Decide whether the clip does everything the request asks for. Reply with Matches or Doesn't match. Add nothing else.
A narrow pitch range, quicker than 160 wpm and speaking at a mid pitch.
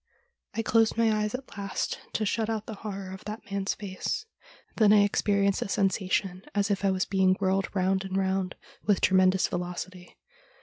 Doesn't match